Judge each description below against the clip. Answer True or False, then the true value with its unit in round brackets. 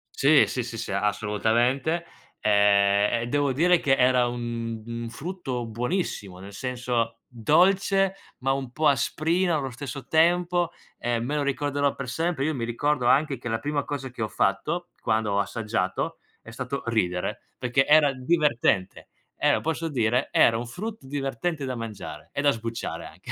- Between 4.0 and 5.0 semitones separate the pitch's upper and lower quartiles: True (4.4 semitones)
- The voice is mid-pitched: False (130 Hz)